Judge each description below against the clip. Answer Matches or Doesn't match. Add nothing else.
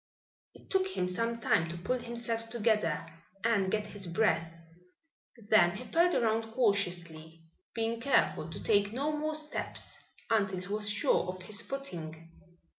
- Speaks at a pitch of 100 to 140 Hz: Doesn't match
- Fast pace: Doesn't match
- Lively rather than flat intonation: Doesn't match